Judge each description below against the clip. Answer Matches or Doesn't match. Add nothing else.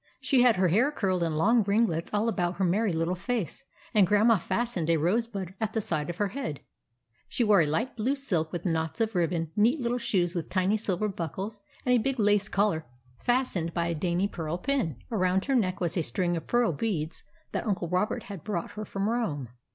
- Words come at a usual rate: Doesn't match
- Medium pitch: Doesn't match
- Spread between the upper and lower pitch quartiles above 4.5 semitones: Matches